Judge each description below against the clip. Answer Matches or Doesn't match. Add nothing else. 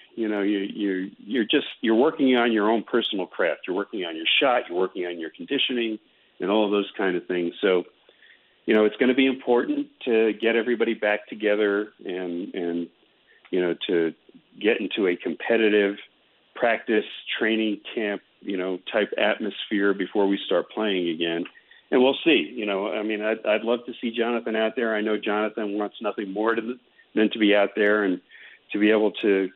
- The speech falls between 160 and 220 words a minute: Matches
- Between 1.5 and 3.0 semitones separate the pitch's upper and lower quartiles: Matches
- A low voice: Matches